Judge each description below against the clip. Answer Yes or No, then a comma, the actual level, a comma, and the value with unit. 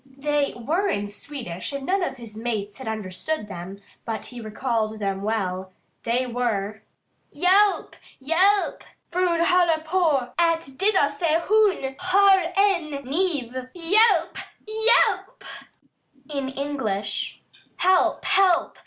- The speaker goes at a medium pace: No, slow, 120 wpm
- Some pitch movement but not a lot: No, wide, 8.6 semitones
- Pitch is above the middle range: Yes, very high, 285 Hz